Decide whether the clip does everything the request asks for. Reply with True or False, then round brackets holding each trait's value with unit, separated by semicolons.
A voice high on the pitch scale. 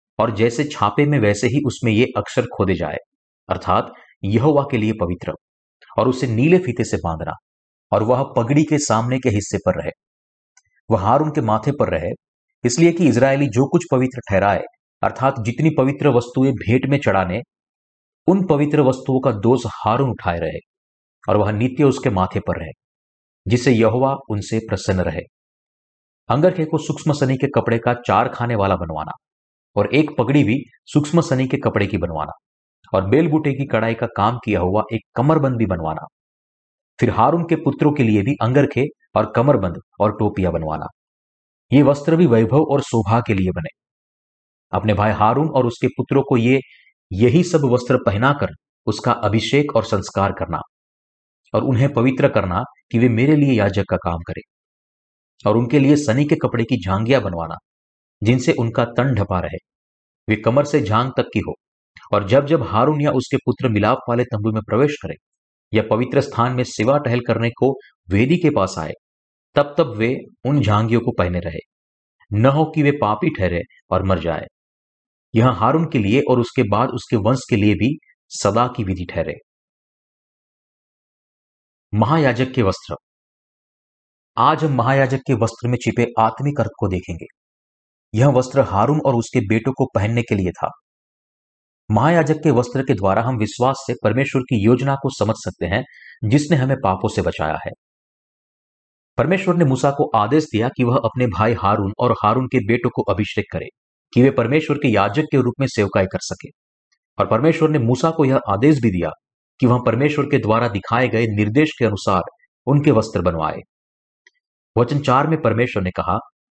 False (120 Hz)